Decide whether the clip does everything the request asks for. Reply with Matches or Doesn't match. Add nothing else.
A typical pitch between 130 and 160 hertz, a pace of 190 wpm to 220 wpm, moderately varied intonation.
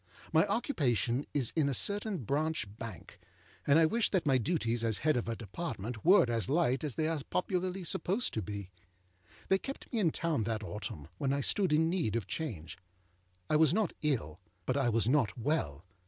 Doesn't match